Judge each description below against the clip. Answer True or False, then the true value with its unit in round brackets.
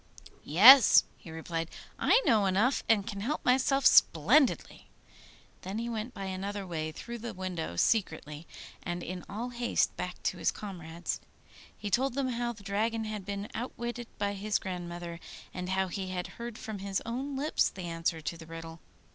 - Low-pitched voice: False (200 Hz)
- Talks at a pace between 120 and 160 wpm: False (170 wpm)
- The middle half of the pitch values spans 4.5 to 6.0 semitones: True (5.1 semitones)